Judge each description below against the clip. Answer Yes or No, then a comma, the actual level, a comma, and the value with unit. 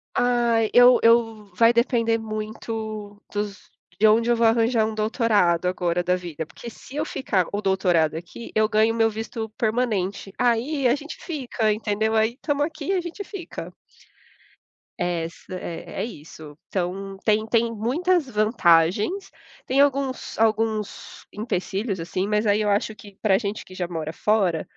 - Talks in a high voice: Yes, high, 220 Hz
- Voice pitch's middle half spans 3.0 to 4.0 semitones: Yes, average, 3.4 semitones